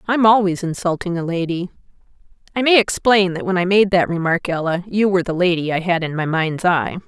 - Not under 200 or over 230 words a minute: Yes, fast, 205 wpm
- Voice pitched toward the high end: No, medium, 180 Hz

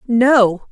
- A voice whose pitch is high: Yes, high, 230 Hz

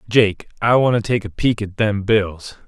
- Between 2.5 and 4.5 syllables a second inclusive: Yes, 4.4 syllables/s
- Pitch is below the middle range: Yes, low, 105 Hz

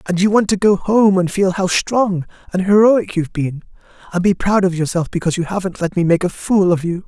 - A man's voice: Yes, male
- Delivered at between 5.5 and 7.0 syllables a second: Yes, 5.7 syllables/s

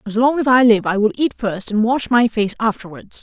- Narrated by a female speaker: Yes, female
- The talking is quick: Yes, fast, 260 wpm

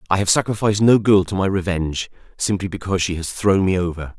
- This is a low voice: Yes, very low, 95 Hz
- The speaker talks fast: Yes, fast, 215 wpm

